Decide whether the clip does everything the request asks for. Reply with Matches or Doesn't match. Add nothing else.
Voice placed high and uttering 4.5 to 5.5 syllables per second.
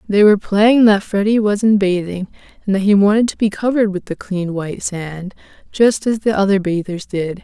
Matches